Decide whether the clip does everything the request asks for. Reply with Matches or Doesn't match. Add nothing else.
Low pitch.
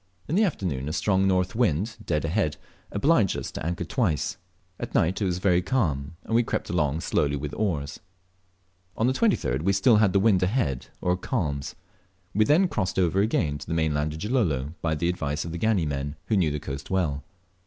Matches